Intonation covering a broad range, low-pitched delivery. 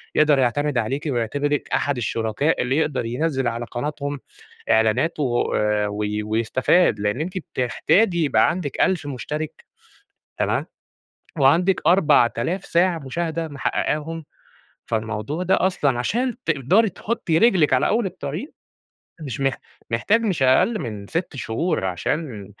No: wide, 6.2 semitones; medium, 145 Hz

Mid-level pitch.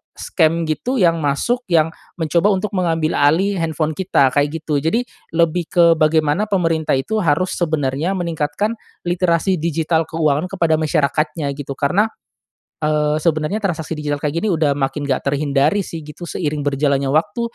Yes: medium, 160 Hz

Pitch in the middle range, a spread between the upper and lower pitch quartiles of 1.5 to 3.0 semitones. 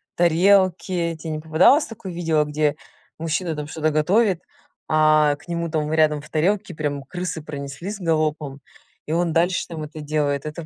Yes: medium, 160 Hz; narrow, 2.5 semitones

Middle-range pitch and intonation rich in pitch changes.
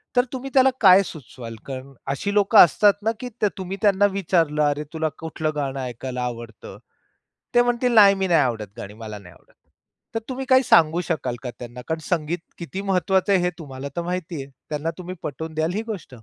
Yes: medium, 165 Hz; wide, 6.6 semitones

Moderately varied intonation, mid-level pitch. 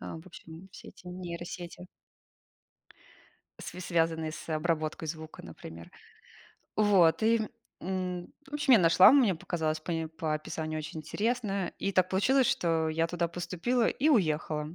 Yes: average, 3.1 semitones; medium, 170 Hz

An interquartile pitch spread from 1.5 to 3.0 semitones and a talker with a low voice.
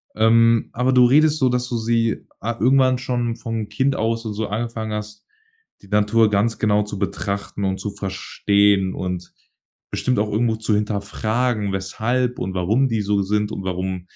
Yes: narrow, 2.6 semitones; low, 110 Hz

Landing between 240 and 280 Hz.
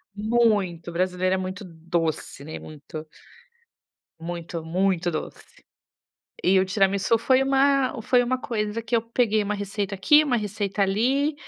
No: high, 200 Hz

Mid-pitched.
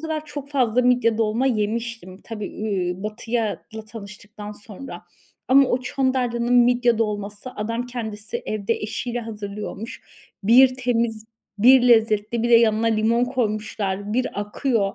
No: high, 230 Hz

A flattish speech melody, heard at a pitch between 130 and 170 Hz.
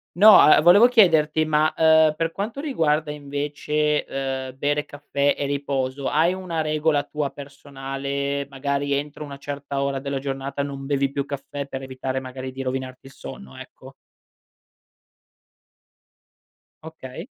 Yes: narrow, 2.0 semitones; medium, 140 Hz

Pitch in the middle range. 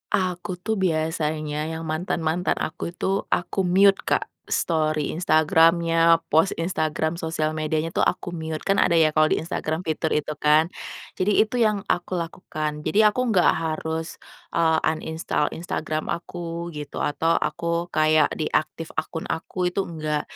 Yes: medium, 160 Hz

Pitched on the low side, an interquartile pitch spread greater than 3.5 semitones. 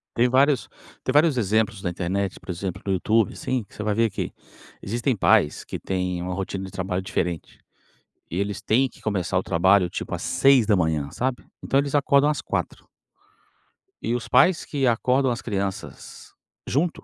Yes: low, 105 Hz; wide, 5.6 semitones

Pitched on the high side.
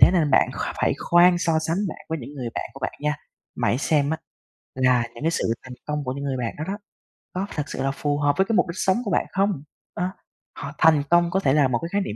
No: medium, 150 Hz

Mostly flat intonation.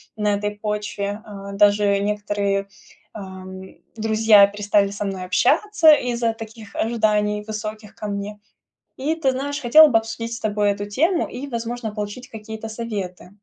Yes: narrow, 2.2 semitones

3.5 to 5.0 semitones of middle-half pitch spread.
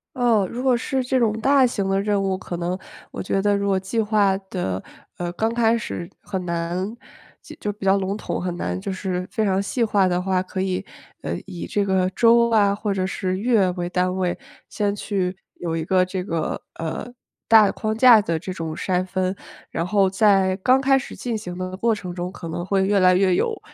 No: average, 2.9 semitones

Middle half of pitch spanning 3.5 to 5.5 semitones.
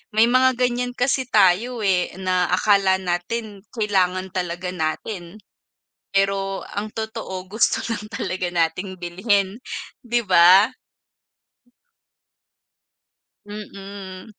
No: average, 3.1 semitones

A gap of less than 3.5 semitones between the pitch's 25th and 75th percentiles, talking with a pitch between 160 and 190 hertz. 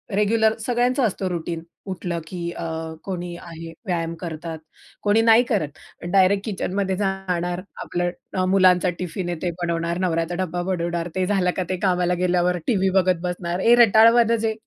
Yes: narrow, 2.6 semitones; medium, 185 Hz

